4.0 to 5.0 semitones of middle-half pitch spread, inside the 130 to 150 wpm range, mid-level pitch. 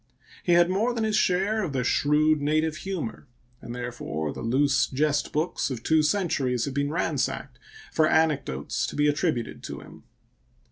No: average, 4.7 semitones; average, 170 wpm; medium, 150 Hz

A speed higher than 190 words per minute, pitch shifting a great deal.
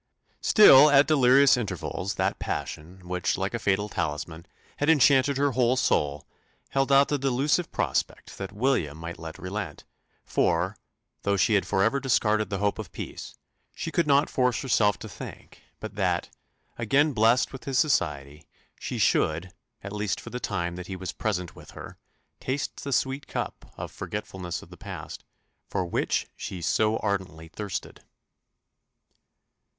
No: average, 160 wpm; wide, 7.0 semitones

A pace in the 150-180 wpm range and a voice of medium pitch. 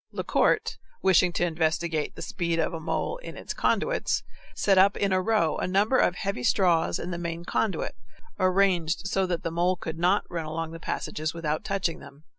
No: average, 195 wpm; medium, 175 Hz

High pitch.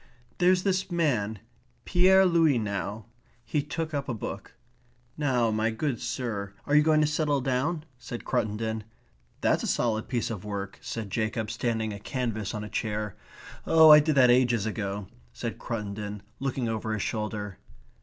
No: low, 115 Hz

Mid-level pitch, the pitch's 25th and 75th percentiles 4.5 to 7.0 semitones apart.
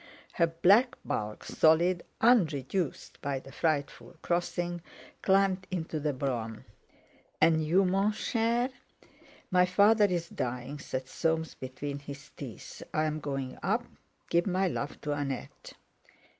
Yes: medium, 165 Hz; average, 4.9 semitones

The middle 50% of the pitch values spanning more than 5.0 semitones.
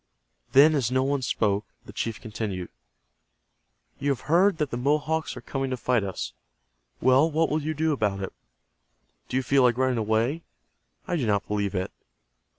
Yes: wide, 5.4 semitones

